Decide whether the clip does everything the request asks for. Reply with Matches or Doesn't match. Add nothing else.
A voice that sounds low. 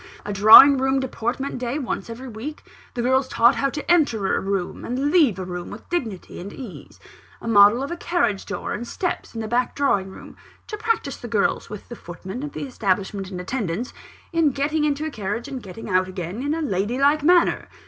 Doesn't match